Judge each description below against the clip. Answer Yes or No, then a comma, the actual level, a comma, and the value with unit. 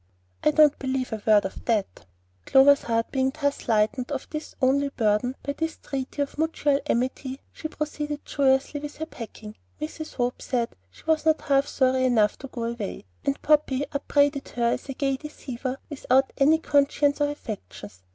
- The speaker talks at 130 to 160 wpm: No, average, 175 wpm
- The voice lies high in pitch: Yes, very high, 275 Hz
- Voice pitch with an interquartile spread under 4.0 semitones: Yes, average, 3.0 semitones